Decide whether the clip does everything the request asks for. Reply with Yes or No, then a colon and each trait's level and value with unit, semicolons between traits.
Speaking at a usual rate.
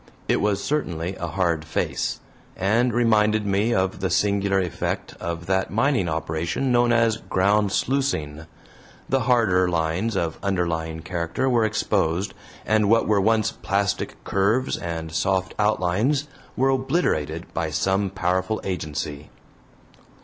No: slow, 130 wpm